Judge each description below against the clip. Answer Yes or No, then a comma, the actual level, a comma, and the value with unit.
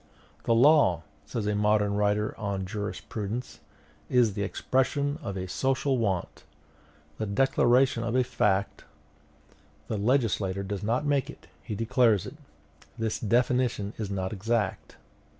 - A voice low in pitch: Yes, low, 110 Hz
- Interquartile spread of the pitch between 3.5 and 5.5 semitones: Yes, average, 3.8 semitones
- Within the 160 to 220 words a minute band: No, slow, 135 wpm